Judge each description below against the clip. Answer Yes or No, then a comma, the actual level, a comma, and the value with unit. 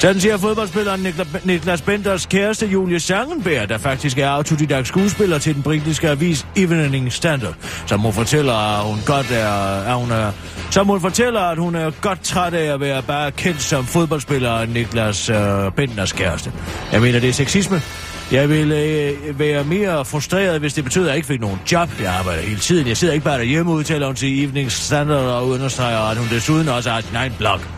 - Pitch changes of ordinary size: No, wide, 6.9 semitones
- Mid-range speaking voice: Yes, medium, 145 Hz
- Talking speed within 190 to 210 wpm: Yes, average, 200 wpm